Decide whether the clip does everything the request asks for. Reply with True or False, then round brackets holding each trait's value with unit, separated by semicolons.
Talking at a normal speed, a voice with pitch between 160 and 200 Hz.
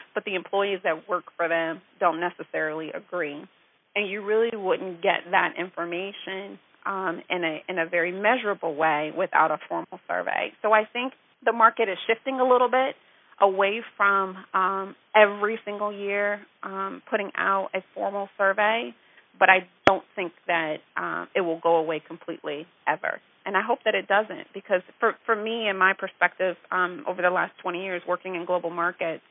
True (175 wpm; 190 Hz)